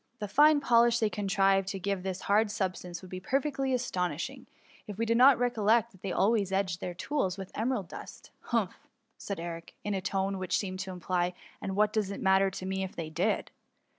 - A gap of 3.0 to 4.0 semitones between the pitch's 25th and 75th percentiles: Yes, average, 3.4 semitones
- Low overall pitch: No, high, 195 Hz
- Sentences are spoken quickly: Yes, fast, 220 wpm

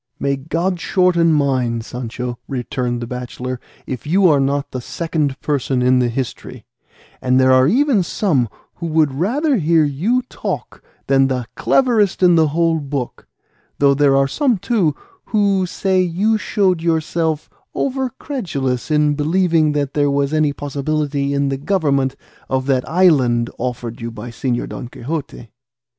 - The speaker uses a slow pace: No, average, 150 wpm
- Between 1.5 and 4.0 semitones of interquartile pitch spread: No, average, 4.8 semitones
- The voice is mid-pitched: Yes, medium, 145 Hz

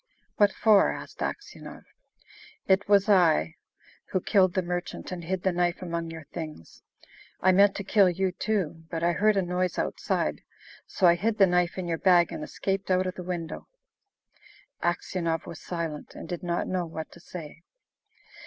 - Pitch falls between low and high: Yes, medium, 180 Hz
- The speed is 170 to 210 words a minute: Yes, average, 175 wpm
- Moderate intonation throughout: No, narrow, 2.0 semitones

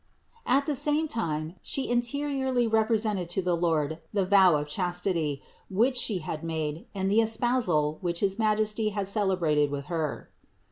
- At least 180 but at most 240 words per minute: No, average, 155 wpm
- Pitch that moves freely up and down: Yes, wide, 5.8 semitones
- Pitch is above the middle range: Yes, high, 195 Hz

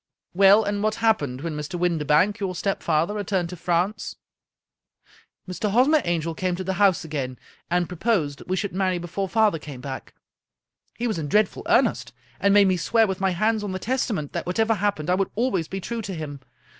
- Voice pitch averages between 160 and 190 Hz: Yes, medium, 185 Hz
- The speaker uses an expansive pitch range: No, average, 3.7 semitones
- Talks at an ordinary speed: No, fast, 210 wpm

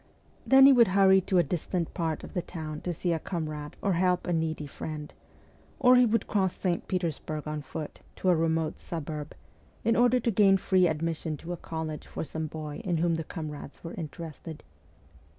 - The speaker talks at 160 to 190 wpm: No, average, 200 wpm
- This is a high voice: No, medium, 165 Hz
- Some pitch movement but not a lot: Yes, average, 3.3 semitones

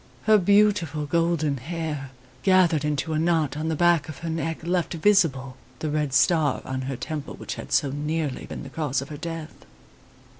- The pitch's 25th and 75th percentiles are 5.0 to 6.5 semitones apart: No, average, 2.8 semitones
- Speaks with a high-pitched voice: No, medium, 155 Hz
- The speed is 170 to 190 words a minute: Yes, average, 185 wpm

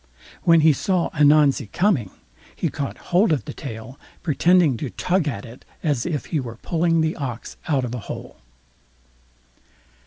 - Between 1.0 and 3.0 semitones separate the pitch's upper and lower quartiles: No, average, 4.7 semitones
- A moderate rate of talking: Yes, average, 160 wpm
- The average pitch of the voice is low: No, medium, 150 Hz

